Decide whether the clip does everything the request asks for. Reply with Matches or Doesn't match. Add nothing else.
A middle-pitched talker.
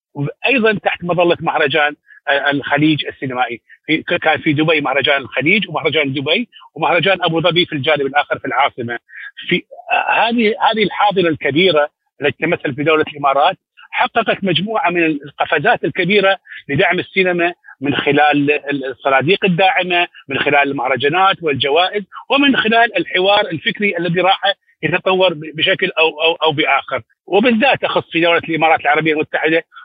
Matches